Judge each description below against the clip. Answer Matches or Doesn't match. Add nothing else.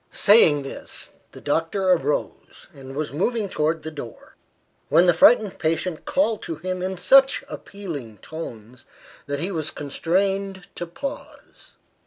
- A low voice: Doesn't match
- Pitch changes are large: Doesn't match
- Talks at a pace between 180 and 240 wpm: Doesn't match